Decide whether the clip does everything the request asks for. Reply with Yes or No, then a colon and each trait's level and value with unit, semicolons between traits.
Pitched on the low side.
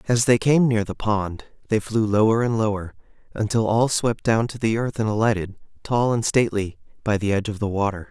Yes: low, 110 Hz